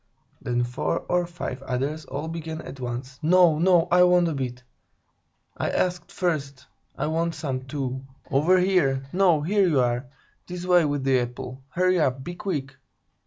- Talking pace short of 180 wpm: Yes, average, 165 wpm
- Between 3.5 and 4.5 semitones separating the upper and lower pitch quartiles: No, average, 5.1 semitones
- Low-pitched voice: No, medium, 150 Hz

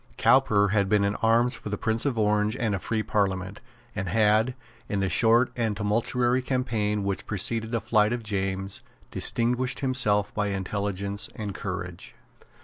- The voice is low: Yes, low, 105 Hz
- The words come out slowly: No, average, 160 wpm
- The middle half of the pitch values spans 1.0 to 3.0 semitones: Yes, narrow, 2.6 semitones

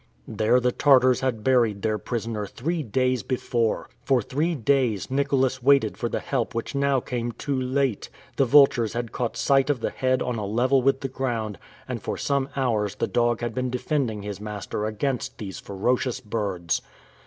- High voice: No, low, 125 Hz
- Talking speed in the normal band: Yes, average, 180 wpm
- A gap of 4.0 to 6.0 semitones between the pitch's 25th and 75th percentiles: No, average, 3.4 semitones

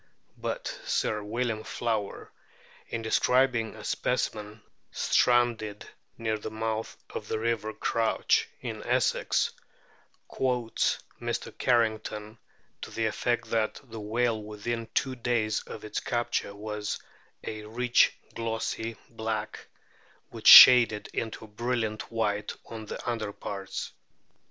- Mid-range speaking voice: No, low, 110 Hz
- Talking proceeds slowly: Yes, slow, 120 wpm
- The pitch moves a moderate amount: No, narrow, 1.7 semitones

